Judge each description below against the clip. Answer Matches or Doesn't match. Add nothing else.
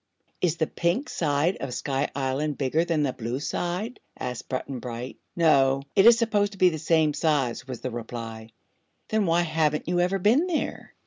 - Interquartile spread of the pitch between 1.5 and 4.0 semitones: Doesn't match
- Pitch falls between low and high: Matches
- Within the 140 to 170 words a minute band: Doesn't match